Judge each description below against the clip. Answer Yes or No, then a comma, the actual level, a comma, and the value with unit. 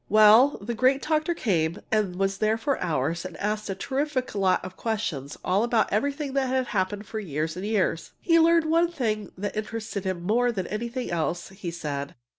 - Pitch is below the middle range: No, high, 215 Hz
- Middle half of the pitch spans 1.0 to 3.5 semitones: No, wide, 5.6 semitones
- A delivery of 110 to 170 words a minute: No, average, 195 wpm